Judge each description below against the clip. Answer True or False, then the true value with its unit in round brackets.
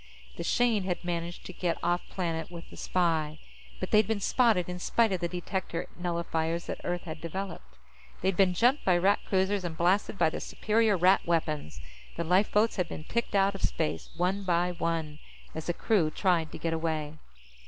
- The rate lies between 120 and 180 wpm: False (190 wpm)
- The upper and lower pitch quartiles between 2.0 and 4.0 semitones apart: True (2.8 semitones)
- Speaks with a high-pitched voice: False (175 Hz)